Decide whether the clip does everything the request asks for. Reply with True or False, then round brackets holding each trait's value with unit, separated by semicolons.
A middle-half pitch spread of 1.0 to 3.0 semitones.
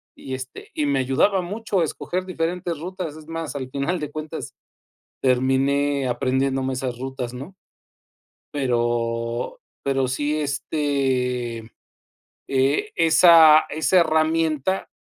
False (3.7 semitones)